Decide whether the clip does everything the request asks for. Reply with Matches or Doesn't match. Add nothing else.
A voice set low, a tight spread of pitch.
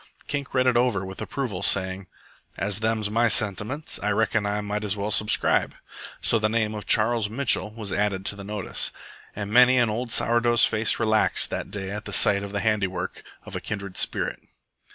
Matches